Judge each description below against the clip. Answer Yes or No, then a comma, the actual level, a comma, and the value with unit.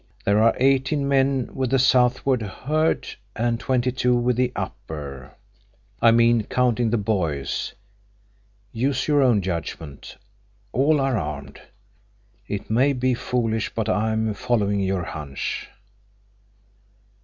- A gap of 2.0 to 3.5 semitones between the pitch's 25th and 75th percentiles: No, average, 4.2 semitones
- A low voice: Yes, low, 120 Hz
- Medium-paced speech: No, slow, 120 wpm